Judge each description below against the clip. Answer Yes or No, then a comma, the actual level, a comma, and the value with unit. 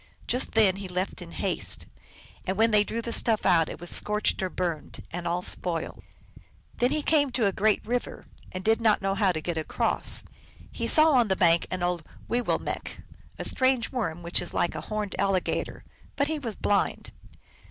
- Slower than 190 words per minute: No, average, 200 wpm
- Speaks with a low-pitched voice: No, high, 200 Hz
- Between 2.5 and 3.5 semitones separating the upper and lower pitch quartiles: No, average, 4.8 semitones